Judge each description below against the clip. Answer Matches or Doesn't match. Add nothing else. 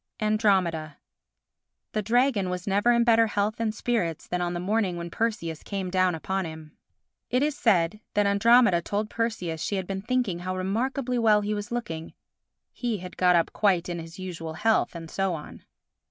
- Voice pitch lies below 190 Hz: Doesn't match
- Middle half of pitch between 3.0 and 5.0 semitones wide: Matches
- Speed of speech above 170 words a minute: Matches